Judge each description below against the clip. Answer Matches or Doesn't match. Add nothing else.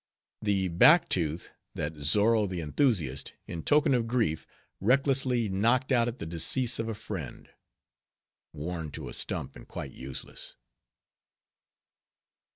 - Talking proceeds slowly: Matches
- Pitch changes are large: Matches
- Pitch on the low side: Matches